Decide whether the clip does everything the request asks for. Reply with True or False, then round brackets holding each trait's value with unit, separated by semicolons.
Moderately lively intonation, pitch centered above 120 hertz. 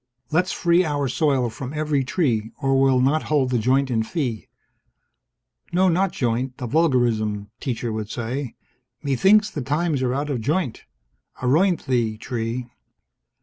True (4.3 semitones; 135 Hz)